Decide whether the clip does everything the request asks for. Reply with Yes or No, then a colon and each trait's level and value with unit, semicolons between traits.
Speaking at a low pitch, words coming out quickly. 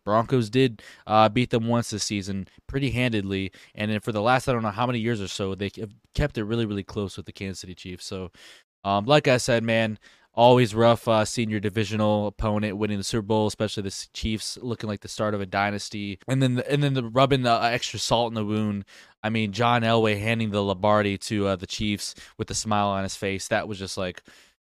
Yes: low, 110 Hz; fast, 230 wpm